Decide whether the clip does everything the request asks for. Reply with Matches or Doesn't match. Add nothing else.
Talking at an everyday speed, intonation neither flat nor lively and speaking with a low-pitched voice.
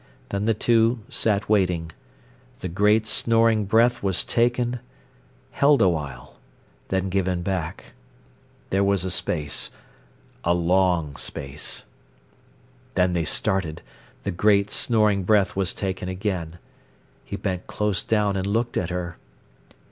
Doesn't match